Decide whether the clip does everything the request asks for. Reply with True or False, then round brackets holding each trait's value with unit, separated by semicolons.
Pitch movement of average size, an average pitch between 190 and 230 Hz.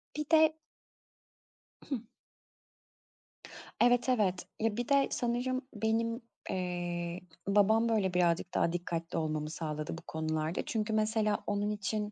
True (4.9 semitones; 205 Hz)